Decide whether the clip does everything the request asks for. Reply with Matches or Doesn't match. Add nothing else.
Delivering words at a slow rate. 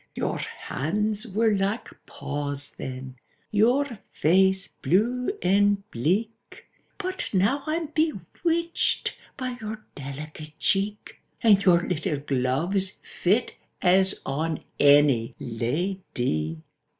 Matches